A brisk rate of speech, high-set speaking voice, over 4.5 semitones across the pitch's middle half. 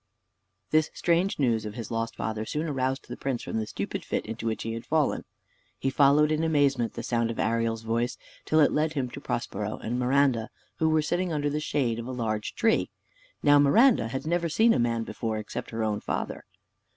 No: fast, 210 wpm; low, 130 Hz; average, 5.0 semitones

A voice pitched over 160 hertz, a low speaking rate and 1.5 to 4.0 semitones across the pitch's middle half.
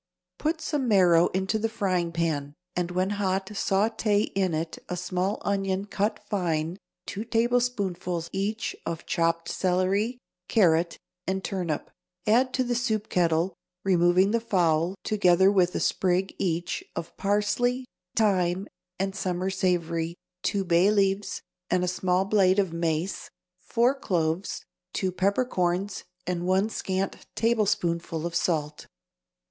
Yes: high, 190 Hz; slow, 130 wpm; average, 2.9 semitones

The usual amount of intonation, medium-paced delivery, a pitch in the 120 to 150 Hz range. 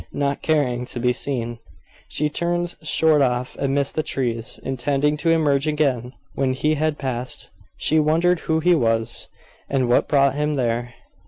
Yes: average, 3.7 semitones; average, 160 wpm; medium, 140 Hz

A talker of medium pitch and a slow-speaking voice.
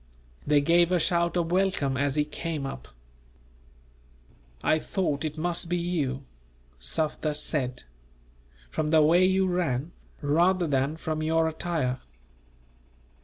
Yes: medium, 160 Hz; slow, 125 wpm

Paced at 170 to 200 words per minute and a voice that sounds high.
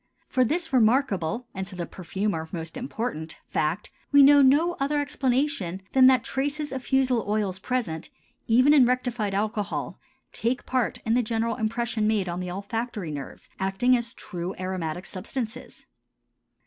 No: average, 150 wpm; high, 225 Hz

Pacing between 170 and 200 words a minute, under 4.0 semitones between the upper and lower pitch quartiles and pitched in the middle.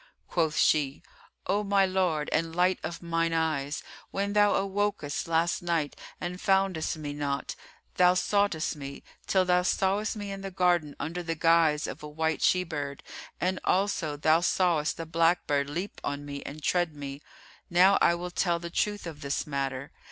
Yes: average, 175 wpm; average, 3.6 semitones; medium, 170 Hz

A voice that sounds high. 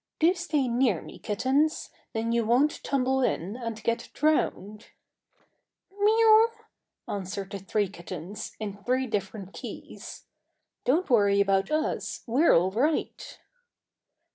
Yes: high, 230 Hz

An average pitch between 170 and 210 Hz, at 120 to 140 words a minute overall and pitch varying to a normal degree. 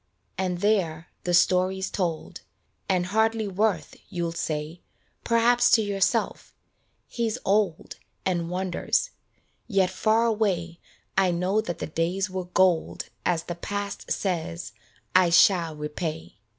Yes: medium, 185 Hz; slow, 135 wpm; average, 3.1 semitones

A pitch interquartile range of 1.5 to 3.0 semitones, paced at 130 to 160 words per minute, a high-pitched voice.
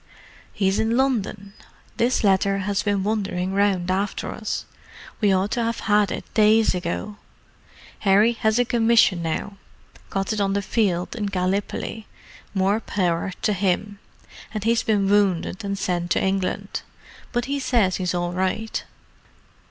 Yes: narrow, 2.5 semitones; average, 145 wpm; high, 200 Hz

